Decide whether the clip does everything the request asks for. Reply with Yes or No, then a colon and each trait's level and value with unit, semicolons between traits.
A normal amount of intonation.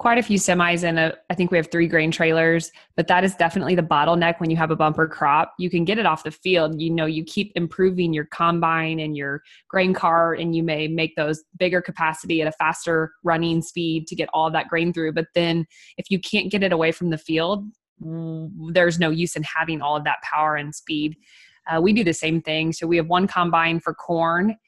No: narrow, 1.7 semitones